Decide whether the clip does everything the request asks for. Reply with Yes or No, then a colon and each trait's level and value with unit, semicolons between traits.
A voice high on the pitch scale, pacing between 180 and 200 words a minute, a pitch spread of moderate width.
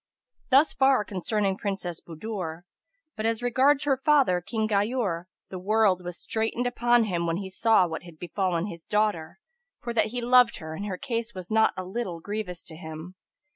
Yes: high, 205 Hz; average, 185 wpm; average, 4.7 semitones